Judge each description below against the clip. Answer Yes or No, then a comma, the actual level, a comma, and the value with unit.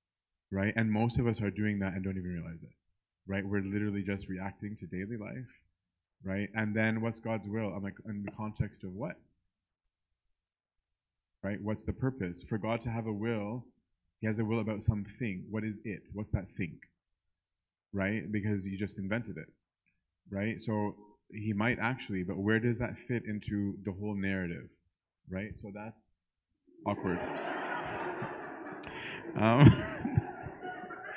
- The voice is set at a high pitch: No, low, 105 Hz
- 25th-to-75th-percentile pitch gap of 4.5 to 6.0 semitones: No, average, 2.8 semitones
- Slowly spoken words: No, average, 155 wpm